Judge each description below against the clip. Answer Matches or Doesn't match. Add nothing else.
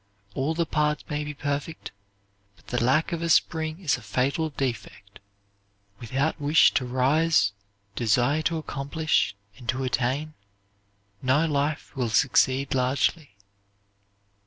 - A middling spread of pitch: Matches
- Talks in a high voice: Doesn't match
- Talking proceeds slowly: Matches